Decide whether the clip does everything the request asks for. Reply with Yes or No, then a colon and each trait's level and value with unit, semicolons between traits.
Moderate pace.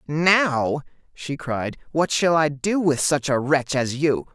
Yes: average, 180 wpm